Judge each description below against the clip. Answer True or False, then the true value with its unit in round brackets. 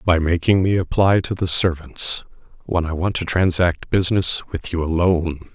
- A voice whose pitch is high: False (85 Hz)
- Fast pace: False (175 wpm)